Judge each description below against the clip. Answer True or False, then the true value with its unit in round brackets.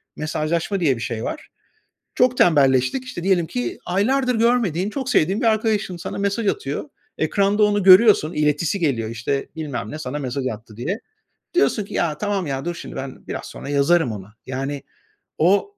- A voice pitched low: False (170 Hz)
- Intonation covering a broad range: True (7.0 semitones)